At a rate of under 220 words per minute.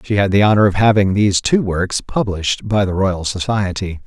Yes: fast, 205 wpm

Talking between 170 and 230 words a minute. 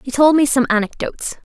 Yes: average, 200 wpm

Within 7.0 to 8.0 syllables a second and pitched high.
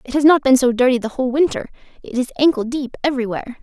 Yes: 7.4 syllables/s; very high, 260 Hz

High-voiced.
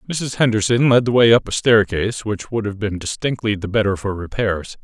No: low, 110 Hz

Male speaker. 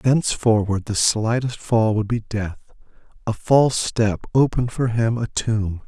Yes: male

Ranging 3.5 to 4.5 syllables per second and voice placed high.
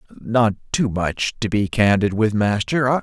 No: 4.2 syllables/s; low, 110 Hz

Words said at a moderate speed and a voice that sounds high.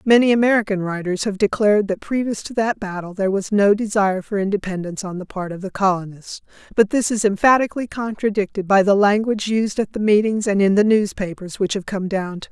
No: fast, 210 wpm; high, 205 Hz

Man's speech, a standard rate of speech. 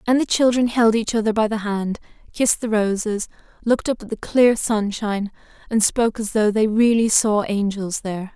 No: female; average, 195 wpm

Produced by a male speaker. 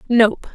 No: female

